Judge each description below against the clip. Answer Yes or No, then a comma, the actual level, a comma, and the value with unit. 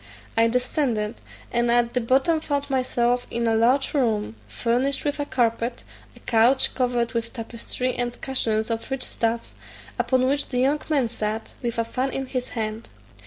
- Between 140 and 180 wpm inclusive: Yes, average, 170 wpm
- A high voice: Yes, high, 245 Hz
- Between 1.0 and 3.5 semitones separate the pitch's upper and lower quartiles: Yes, narrow, 2.4 semitones